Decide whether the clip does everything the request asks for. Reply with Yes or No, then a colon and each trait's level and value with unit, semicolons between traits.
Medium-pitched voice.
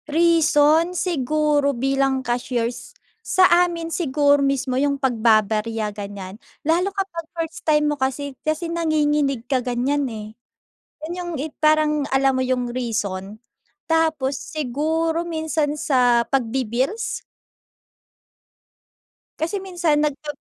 No: very high, 290 Hz